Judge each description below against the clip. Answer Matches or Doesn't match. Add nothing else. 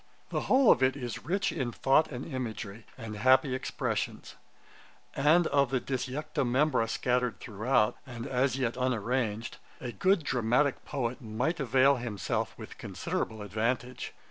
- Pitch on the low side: Matches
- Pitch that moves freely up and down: Doesn't match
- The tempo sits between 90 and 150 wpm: Matches